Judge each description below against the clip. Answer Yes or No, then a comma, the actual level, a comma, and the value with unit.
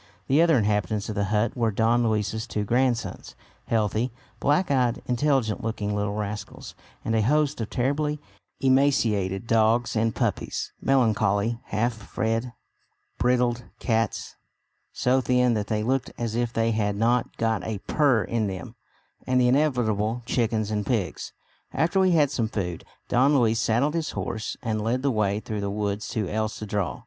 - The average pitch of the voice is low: Yes, low, 115 Hz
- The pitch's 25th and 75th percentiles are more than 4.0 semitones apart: No, average, 3.0 semitones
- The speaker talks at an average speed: Yes, average, 165 wpm